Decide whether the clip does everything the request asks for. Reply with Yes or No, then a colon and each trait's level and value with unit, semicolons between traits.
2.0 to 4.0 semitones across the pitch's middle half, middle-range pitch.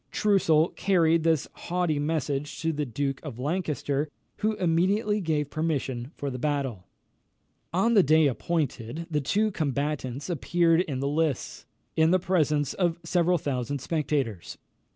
Yes: average, 3.6 semitones; medium, 155 Hz